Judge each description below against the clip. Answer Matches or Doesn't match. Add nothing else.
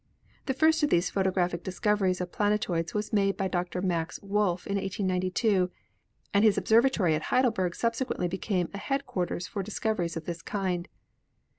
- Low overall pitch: Doesn't match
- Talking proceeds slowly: Doesn't match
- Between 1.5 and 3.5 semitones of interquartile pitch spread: Matches